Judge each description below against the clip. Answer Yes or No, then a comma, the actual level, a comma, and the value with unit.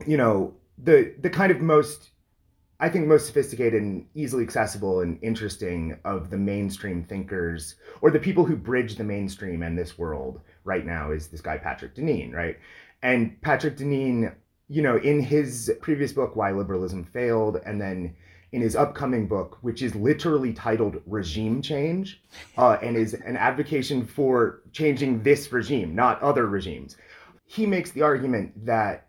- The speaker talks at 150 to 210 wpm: Yes, average, 165 wpm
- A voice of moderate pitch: No, low, 115 Hz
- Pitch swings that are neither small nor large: No, wide, 7.2 semitones